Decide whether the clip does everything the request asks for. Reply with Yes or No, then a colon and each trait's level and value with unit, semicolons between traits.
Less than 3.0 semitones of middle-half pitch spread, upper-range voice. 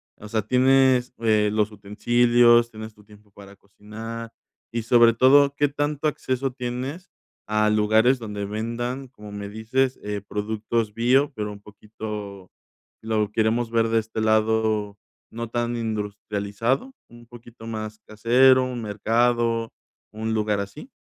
No: narrow, 2.4 semitones; low, 115 Hz